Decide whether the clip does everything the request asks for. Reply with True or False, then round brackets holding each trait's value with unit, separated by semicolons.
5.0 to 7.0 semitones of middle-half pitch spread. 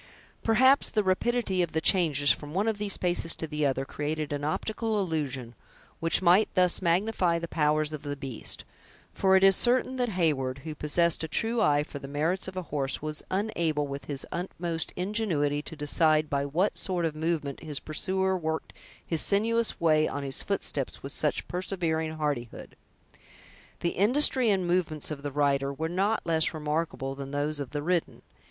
False (4.3 semitones)